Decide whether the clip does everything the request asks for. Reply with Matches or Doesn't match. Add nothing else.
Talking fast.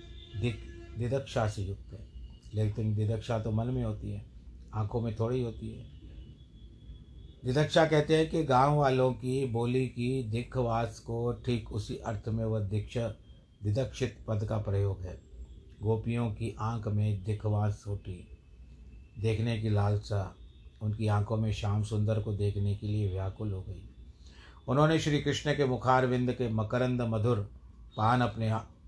Doesn't match